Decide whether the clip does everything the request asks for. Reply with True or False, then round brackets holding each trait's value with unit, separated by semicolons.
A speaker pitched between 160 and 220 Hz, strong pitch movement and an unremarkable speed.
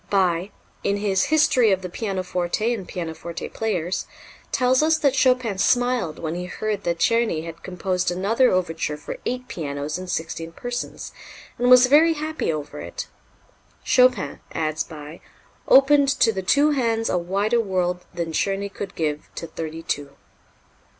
True (190 Hz; 6.6 semitones; 155 wpm)